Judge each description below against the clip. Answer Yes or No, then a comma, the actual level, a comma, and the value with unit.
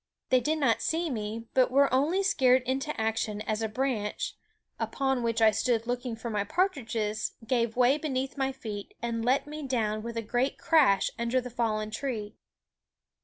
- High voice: Yes, high, 245 Hz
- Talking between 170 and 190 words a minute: Yes, average, 175 wpm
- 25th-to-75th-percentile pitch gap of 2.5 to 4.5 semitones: Yes, average, 3.3 semitones